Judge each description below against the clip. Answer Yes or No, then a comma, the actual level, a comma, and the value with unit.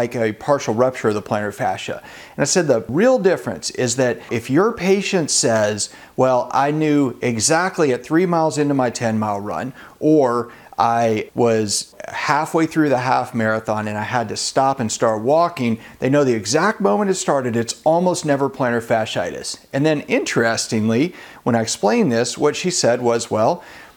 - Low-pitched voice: Yes, low, 125 Hz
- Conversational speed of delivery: Yes, average, 180 wpm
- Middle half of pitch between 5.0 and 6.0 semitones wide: Yes, wide, 5.4 semitones